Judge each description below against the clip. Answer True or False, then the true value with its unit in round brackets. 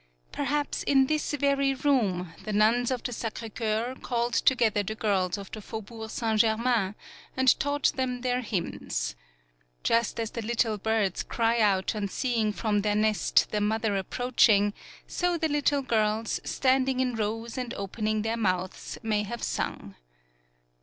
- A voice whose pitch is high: True (225 Hz)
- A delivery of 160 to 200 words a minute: True (165 wpm)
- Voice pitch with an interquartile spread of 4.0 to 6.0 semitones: False (3.2 semitones)